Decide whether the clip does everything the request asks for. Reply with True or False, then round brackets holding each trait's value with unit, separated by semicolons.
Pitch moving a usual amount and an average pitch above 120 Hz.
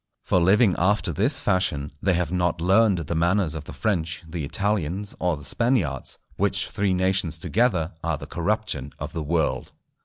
False (3.9 semitones; 90 Hz)